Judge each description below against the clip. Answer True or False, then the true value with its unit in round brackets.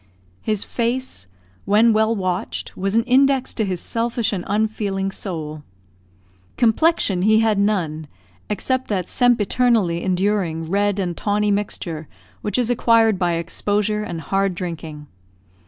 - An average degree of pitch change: True (3.8 semitones)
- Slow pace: True (130 wpm)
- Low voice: False (205 Hz)